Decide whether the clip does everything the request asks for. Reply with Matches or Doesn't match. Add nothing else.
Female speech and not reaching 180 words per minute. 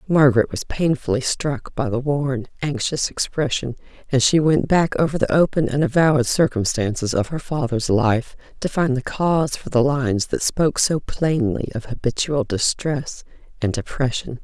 Matches